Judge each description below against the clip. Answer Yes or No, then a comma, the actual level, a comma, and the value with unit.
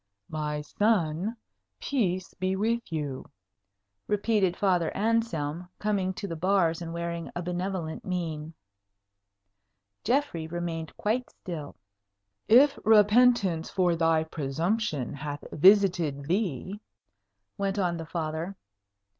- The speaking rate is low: Yes, slow, 110 wpm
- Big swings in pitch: No, average, 4.2 semitones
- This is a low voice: No, medium, 175 Hz